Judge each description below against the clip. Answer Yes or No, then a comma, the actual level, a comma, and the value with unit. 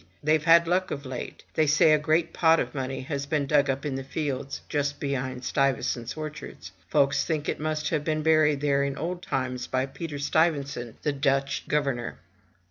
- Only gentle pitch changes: Yes, narrow, 2.2 semitones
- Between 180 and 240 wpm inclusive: Yes, average, 200 wpm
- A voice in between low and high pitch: Yes, medium, 145 Hz